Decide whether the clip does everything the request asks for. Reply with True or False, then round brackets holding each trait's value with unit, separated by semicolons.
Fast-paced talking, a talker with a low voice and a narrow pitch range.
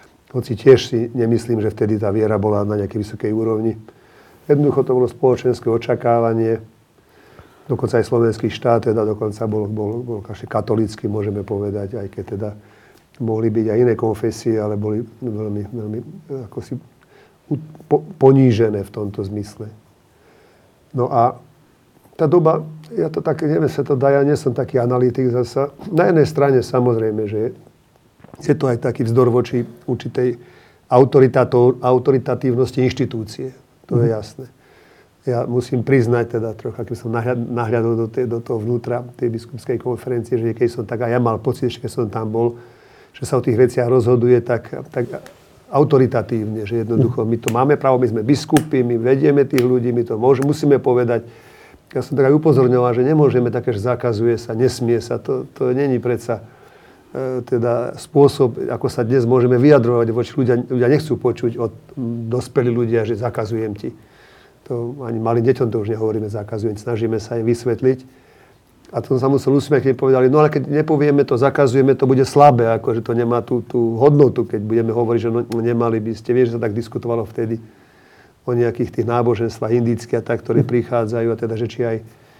True (175 wpm; 120 Hz; 2.2 semitones)